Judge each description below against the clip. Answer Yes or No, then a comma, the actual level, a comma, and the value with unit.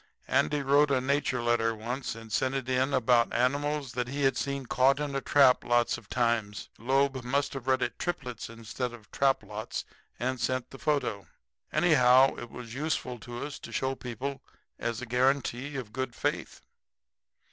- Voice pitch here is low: Yes, low, 130 Hz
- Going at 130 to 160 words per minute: No, average, 180 wpm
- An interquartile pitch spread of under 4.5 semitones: Yes, narrow, 2.5 semitones